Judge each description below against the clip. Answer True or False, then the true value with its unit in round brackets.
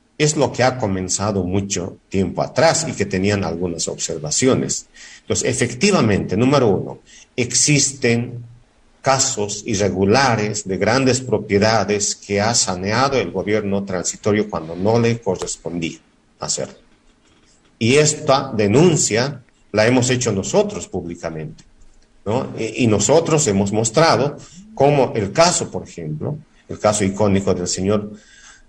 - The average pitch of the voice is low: True (105 Hz)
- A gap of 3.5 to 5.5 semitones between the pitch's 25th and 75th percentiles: True (4.7 semitones)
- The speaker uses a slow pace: True (120 wpm)